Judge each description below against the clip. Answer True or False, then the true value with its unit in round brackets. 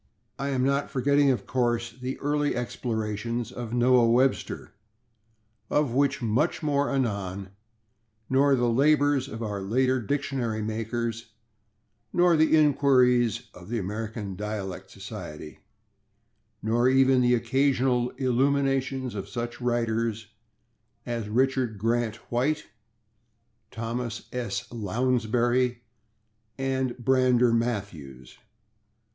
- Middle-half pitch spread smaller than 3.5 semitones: True (3.0 semitones)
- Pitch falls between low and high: False (120 Hz)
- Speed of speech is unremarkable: False (105 wpm)